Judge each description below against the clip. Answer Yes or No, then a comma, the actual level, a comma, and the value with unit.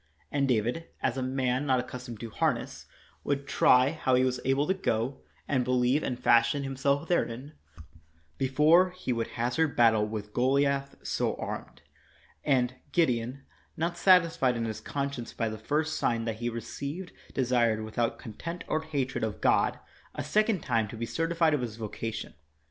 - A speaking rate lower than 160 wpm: No, average, 165 wpm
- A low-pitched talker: Yes, low, 130 Hz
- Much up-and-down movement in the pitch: No, average, 3.9 semitones